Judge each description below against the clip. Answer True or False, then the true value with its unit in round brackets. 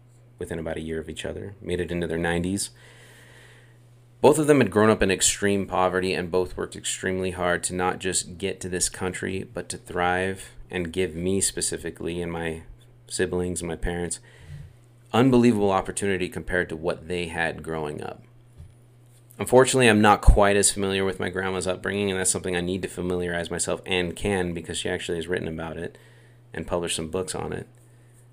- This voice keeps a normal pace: True (185 wpm)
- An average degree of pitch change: True (4.5 semitones)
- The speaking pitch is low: True (95 Hz)